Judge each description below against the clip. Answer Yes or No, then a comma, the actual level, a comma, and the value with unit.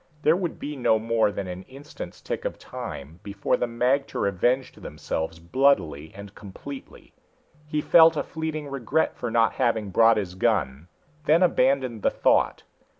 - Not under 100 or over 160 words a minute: Yes, average, 155 wpm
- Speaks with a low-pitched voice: Yes, low, 115 Hz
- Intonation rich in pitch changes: Yes, wide, 6.2 semitones